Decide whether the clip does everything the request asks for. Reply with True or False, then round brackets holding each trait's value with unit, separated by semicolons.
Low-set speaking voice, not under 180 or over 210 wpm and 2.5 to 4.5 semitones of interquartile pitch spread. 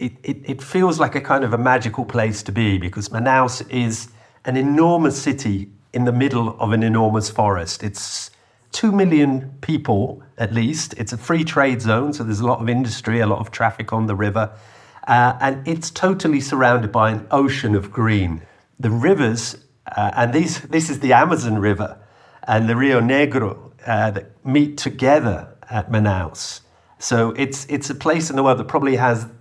True (120 Hz; 190 wpm; 3.9 semitones)